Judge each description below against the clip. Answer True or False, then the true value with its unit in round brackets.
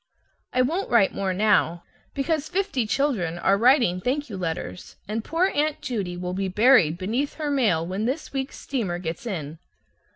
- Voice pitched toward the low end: False (220 Hz)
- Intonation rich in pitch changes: True (7.2 semitones)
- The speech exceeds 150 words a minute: True (170 wpm)